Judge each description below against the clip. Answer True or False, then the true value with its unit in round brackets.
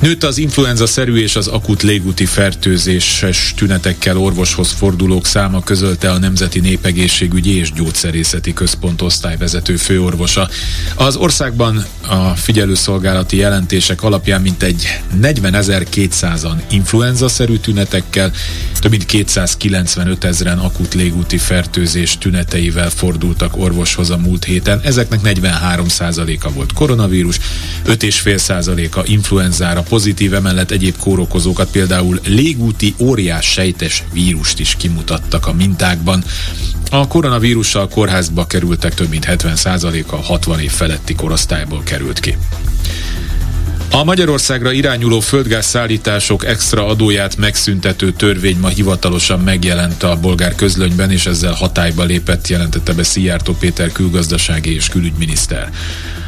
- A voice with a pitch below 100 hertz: True (90 Hz)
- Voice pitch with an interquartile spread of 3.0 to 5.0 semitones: False (2.6 semitones)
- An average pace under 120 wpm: True (110 wpm)